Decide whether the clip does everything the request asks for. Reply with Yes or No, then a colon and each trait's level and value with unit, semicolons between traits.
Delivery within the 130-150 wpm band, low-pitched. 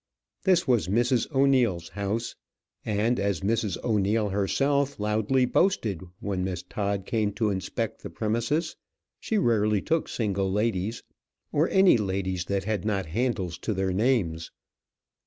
Yes: average, 140 wpm; low, 105 Hz